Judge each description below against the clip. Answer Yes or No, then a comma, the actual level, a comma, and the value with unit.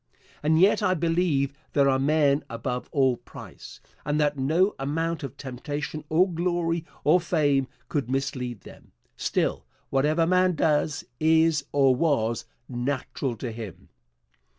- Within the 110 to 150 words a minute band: Yes, slow, 135 wpm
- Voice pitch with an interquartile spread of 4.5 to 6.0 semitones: No, average, 3.5 semitones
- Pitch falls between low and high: Yes, medium, 145 Hz